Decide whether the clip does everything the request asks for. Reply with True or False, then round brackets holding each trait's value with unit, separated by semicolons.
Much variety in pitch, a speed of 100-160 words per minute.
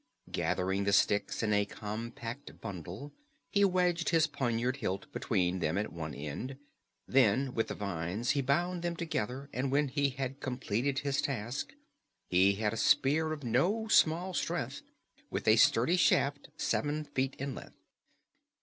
True (5.7 semitones; 155 wpm)